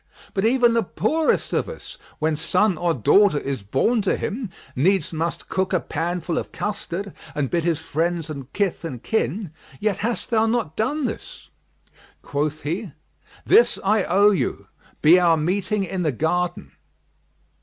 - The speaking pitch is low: No, medium, 180 Hz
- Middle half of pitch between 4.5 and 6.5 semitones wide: Yes, average, 4.9 semitones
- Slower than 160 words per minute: No, average, 165 wpm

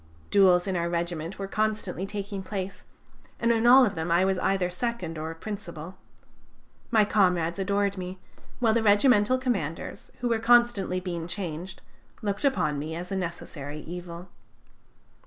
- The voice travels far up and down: No, average, 3.6 semitones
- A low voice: No, high, 190 Hz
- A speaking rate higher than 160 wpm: No, average, 155 wpm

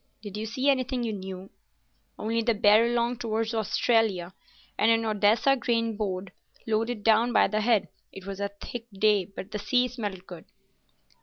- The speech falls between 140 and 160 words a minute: No, average, 170 wpm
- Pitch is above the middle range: Yes, high, 220 Hz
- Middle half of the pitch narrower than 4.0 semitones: Yes, narrow, 2.5 semitones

